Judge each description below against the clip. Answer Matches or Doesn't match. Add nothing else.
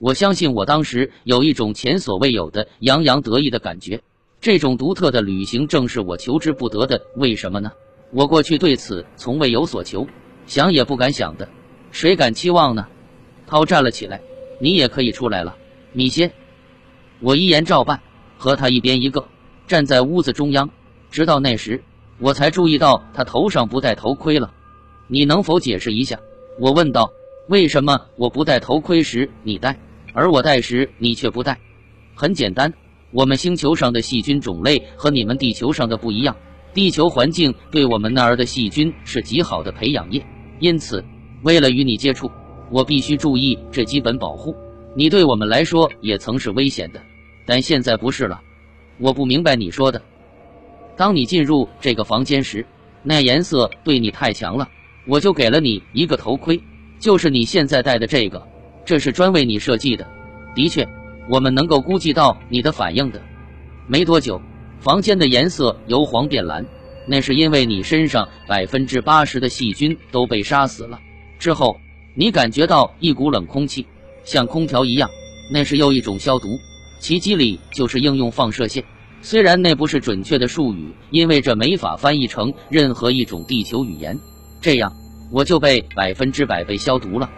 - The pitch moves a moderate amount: Matches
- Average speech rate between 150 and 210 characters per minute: Doesn't match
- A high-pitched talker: Doesn't match